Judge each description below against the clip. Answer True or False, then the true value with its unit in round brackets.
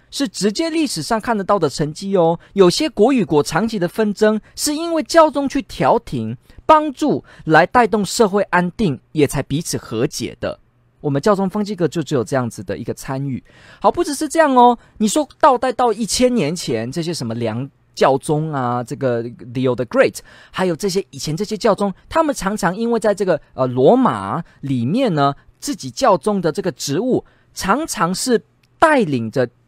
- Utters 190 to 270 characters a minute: False (285 characters per minute)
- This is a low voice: False (180 Hz)